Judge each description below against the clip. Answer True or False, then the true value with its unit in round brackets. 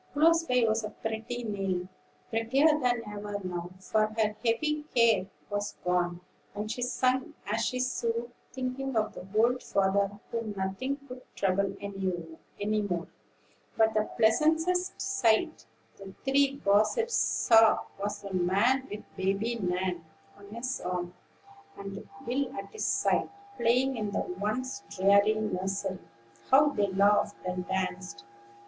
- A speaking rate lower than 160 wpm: True (135 wpm)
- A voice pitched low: False (215 Hz)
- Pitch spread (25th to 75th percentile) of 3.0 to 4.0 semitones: False (4.5 semitones)